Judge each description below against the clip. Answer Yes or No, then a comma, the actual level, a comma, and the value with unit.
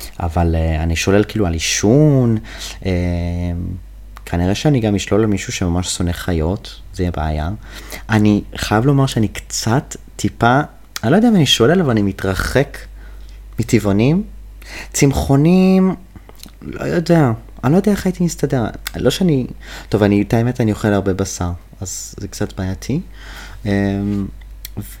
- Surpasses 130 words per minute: Yes, average, 145 wpm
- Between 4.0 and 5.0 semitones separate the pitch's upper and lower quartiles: Yes, average, 4.7 semitones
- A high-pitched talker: No, low, 105 Hz